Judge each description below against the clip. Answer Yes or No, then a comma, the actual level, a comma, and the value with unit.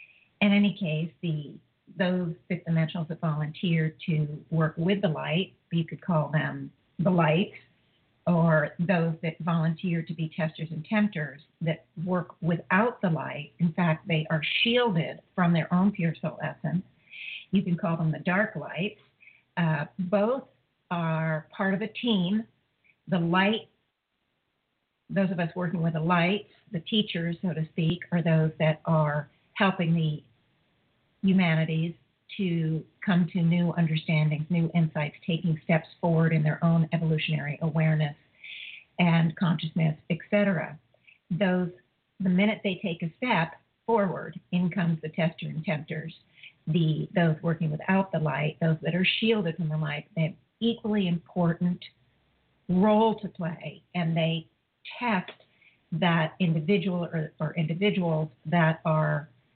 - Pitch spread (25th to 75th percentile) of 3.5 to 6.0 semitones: No, narrow, 2.6 semitones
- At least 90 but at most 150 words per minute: Yes, average, 145 wpm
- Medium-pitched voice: Yes, medium, 165 Hz